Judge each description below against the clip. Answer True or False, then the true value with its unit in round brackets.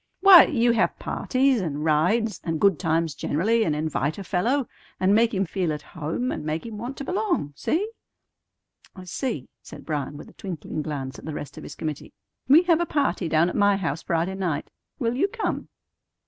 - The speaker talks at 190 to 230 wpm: True (200 wpm)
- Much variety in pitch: True (7.5 semitones)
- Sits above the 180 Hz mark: True (190 Hz)